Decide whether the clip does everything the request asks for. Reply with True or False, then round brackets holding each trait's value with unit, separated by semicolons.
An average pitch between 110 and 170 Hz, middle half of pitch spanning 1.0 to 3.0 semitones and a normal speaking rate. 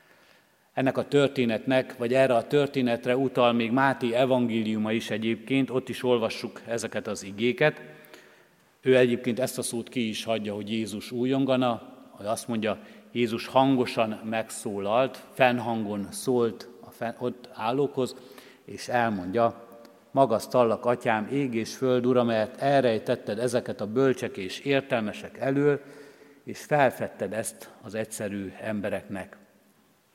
True (120 Hz; 2.6 semitones; 130 wpm)